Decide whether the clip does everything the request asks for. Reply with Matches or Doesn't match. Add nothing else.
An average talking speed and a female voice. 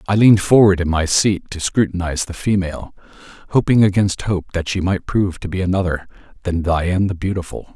Doesn't match